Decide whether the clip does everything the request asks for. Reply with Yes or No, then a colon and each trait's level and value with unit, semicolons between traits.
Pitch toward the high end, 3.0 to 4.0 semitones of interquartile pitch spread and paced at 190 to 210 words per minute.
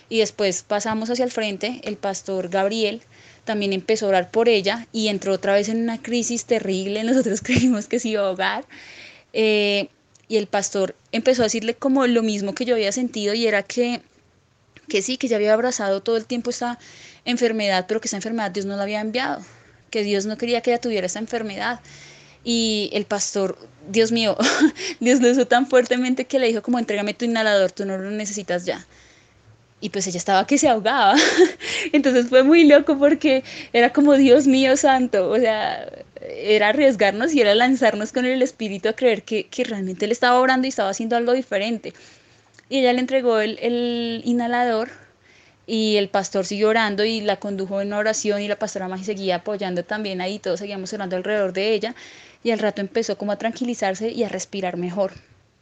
Yes: high, 220 Hz; average, 3.3 semitones; average, 195 wpm